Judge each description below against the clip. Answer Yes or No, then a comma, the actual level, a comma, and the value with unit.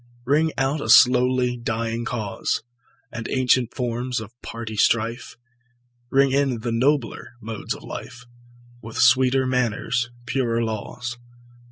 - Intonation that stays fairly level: Yes, narrow, 2.0 semitones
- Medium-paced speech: No, slow, 125 wpm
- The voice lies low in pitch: Yes, low, 120 Hz